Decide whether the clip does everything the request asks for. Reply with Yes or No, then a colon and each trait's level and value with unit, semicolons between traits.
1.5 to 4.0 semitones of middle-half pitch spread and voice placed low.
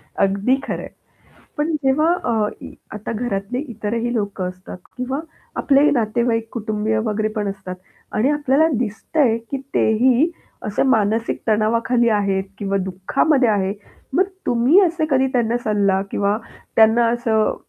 No: average, 3.6 semitones; high, 225 Hz